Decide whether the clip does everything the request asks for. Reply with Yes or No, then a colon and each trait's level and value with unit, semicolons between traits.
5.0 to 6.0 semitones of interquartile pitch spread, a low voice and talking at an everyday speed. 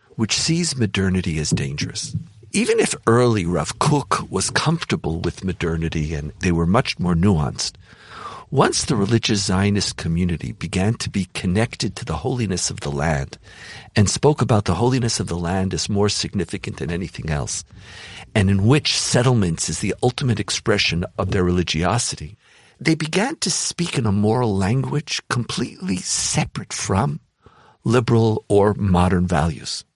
Yes: wide, 5.4 semitones; low, 105 Hz; average, 150 wpm